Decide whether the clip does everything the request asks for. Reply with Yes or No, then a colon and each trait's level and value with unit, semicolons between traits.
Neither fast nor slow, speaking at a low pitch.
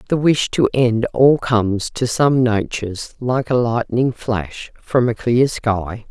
Yes: average, 165 wpm; low, 120 Hz